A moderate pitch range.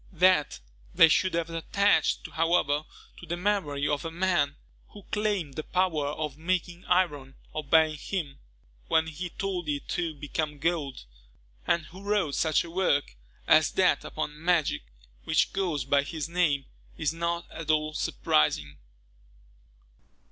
Yes: average, 3.4 semitones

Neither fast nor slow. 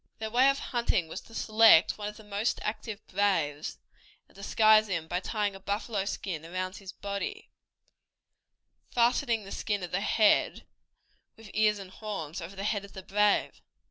Yes: average, 175 wpm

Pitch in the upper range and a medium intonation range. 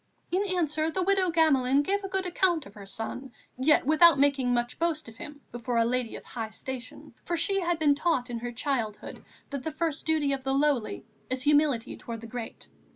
Yes: very high, 280 Hz; average, 4.9 semitones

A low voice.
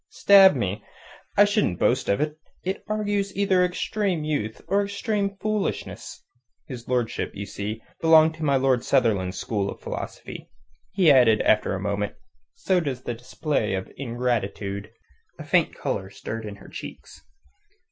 Yes: low, 130 Hz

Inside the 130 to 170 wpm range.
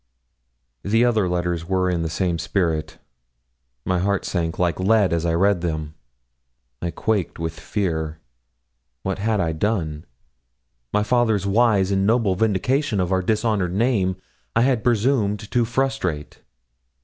Yes: average, 140 wpm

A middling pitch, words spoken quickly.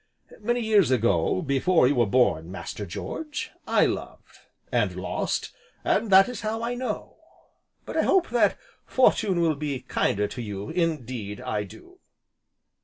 No: medium, 150 Hz; average, 150 wpm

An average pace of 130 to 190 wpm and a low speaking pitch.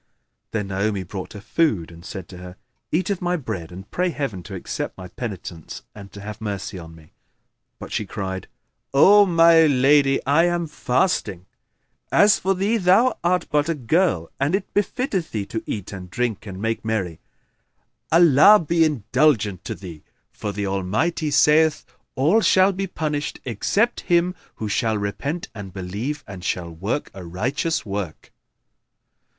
Yes: average, 165 wpm; low, 120 Hz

